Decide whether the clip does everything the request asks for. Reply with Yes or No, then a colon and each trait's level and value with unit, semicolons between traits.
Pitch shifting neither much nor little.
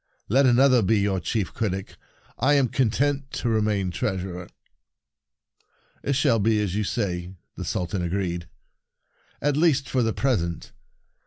No: wide, 5.8 semitones